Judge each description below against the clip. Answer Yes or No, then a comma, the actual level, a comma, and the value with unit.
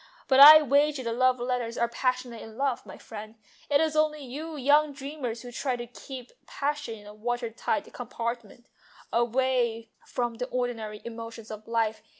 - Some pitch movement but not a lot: Yes, average, 3.3 semitones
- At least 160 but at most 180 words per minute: Yes, average, 165 wpm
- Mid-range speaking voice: No, high, 245 Hz